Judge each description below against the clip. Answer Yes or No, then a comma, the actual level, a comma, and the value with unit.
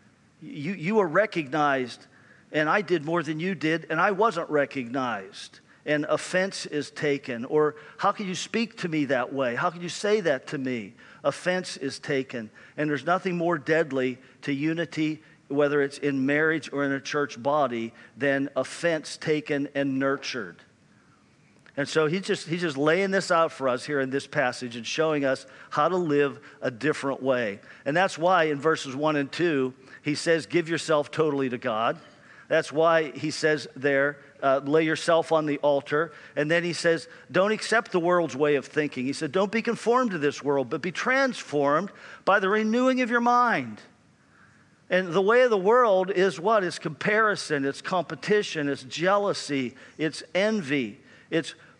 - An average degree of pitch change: Yes, average, 4.2 semitones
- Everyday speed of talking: Yes, average, 180 wpm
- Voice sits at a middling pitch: Yes, medium, 155 Hz